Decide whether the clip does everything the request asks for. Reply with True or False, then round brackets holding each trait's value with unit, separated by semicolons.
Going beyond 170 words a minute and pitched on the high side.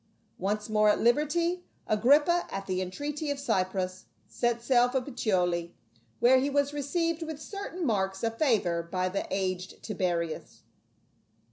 False (140 wpm; 230 Hz)